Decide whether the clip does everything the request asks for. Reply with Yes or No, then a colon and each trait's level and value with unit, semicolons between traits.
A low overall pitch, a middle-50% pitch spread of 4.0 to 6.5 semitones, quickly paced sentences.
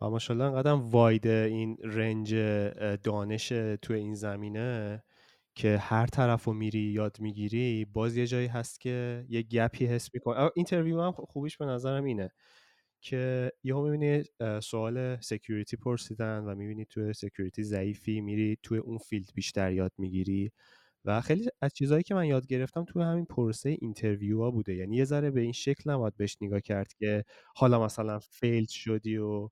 No: low, 115 Hz; average, 3.1 semitones; fast, 165 wpm